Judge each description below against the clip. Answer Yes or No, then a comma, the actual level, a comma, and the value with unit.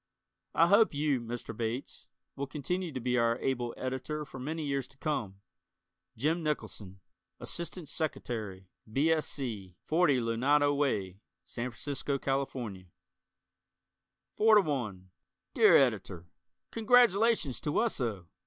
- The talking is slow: Yes, slow, 125 wpm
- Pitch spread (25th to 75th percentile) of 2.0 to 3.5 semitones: No, average, 4.8 semitones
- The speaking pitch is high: No, low, 135 Hz